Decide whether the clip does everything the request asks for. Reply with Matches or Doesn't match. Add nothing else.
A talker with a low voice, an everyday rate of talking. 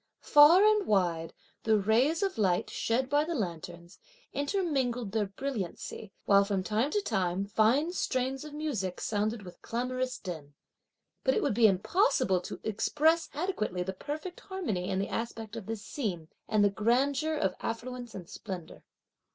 Doesn't match